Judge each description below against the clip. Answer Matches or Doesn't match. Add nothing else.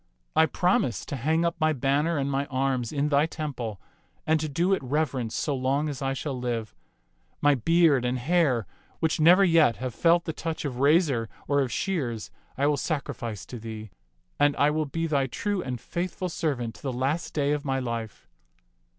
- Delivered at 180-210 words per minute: Matches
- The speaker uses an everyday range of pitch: Matches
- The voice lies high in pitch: Doesn't match